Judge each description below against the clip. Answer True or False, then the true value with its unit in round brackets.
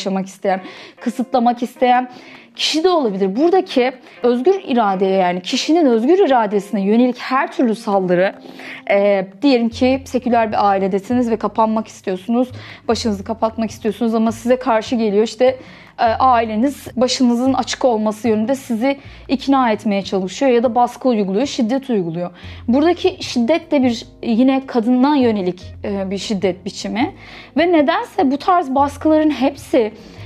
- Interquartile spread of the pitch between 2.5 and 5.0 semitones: True (4.2 semitones)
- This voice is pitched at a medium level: False (240 Hz)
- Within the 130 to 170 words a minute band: True (135 wpm)